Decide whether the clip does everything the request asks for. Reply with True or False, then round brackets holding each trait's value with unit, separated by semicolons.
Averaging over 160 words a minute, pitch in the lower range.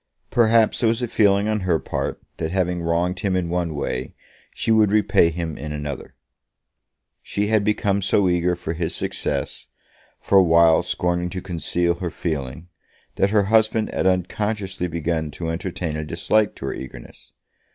True (170 wpm; 90 Hz)